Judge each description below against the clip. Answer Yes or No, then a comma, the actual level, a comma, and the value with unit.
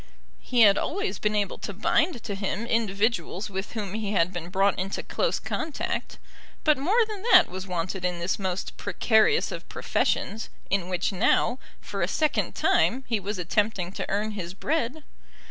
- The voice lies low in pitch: No, high, 205 Hz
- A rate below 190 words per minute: Yes, average, 175 wpm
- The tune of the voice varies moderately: Yes, average, 4.1 semitones